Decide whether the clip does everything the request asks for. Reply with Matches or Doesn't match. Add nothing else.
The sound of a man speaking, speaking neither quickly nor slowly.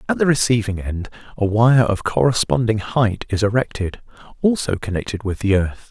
Matches